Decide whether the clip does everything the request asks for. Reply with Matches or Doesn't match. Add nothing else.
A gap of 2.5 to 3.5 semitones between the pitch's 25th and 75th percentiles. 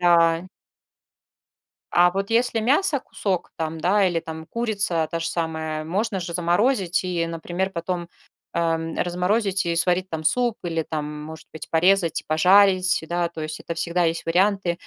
Matches